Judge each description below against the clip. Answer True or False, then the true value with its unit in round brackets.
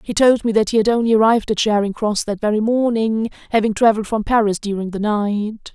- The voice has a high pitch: True (215 Hz)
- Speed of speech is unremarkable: False (220 wpm)